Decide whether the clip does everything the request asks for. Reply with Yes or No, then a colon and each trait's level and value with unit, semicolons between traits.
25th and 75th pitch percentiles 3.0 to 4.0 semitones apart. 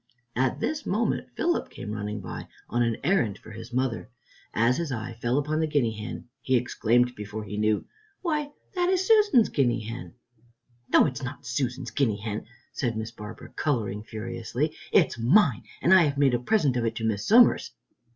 No: average, 5.3 semitones